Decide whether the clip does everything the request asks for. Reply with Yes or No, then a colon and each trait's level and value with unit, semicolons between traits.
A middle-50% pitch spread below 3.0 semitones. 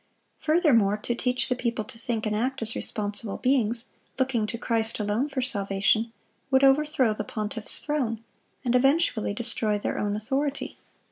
No: average, 3.7 semitones